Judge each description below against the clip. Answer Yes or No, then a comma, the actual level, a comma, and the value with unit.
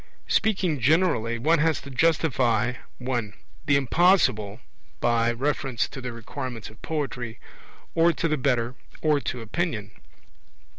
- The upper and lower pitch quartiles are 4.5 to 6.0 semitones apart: Yes, average, 5.2 semitones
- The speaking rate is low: Yes, slow, 130 wpm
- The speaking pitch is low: Yes, low, 130 Hz